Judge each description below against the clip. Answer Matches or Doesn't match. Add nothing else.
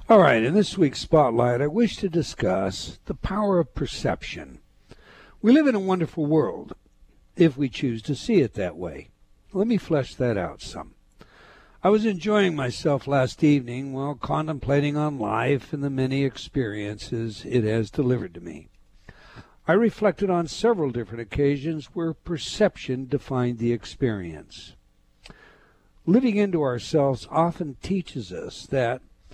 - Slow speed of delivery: Doesn't match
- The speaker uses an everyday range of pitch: Doesn't match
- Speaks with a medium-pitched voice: Matches